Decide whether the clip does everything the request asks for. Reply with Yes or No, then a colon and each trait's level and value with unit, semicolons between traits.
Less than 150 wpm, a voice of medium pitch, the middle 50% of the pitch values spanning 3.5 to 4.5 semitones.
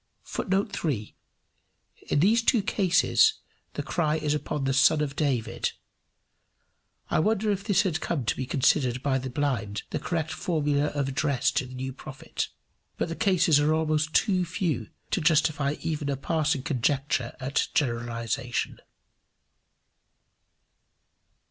Yes: average, 140 wpm; medium, 150 Hz; average, 3.8 semitones